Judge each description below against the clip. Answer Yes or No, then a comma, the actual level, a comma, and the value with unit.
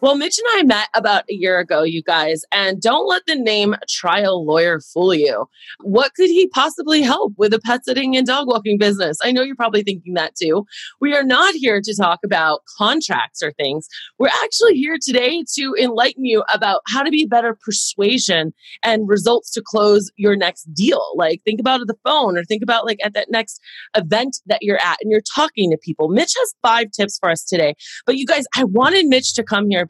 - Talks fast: Yes, fast, 215 wpm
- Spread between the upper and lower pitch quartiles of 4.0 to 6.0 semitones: Yes, average, 4.9 semitones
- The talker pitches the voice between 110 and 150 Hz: No, high, 225 Hz